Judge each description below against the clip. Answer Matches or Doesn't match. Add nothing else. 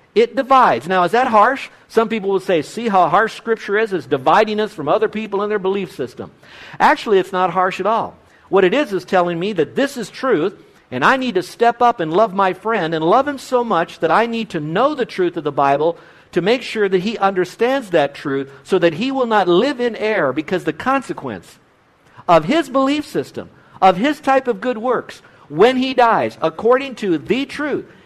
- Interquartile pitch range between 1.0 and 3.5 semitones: Doesn't match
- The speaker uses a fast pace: Matches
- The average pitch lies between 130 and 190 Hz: Doesn't match